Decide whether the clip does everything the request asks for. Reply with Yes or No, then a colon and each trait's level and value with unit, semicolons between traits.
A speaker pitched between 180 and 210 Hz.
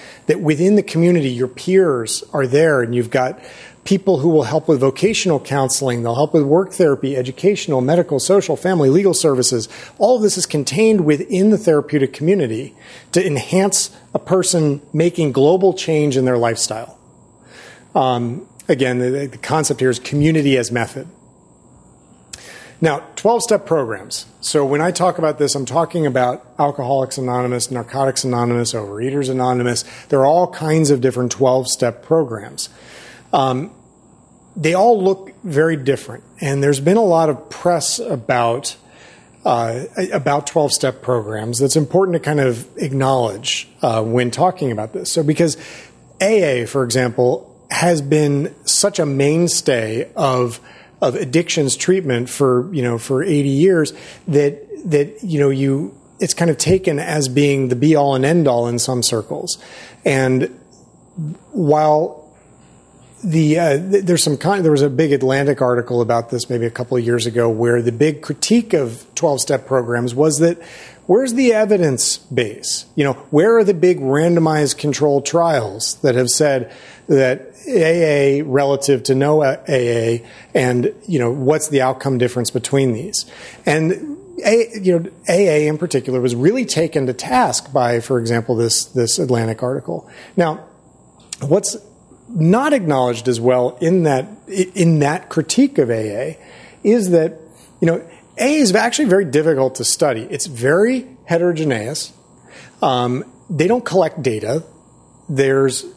No: medium, 145 Hz